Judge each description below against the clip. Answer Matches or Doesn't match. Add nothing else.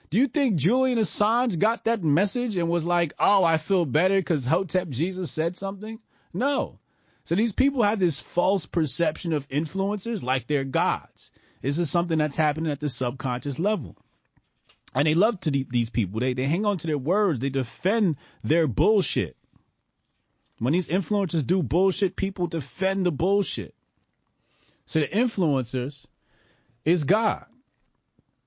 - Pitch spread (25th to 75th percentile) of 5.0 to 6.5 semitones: Matches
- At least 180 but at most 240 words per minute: Doesn't match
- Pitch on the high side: Doesn't match